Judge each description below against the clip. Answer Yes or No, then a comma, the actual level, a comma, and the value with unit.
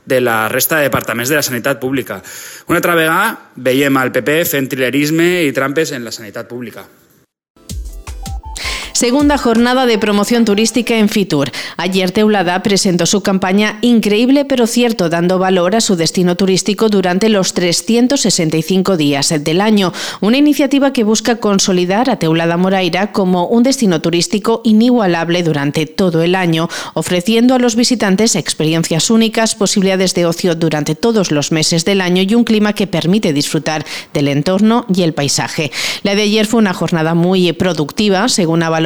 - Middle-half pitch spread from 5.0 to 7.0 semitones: Yes, average, 5.3 semitones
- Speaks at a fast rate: No, average, 160 wpm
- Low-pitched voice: No, medium, 185 Hz